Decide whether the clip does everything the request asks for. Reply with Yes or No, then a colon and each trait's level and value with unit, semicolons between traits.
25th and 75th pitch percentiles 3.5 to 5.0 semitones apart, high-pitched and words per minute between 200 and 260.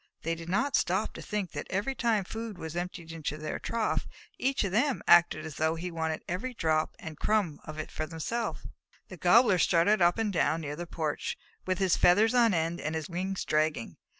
No: average, 4.7 semitones; medium, 175 Hz; fast, 205 wpm